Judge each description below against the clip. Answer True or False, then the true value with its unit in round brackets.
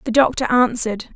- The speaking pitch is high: True (240 Hz)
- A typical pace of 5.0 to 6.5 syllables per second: True (6.0 syllables/s)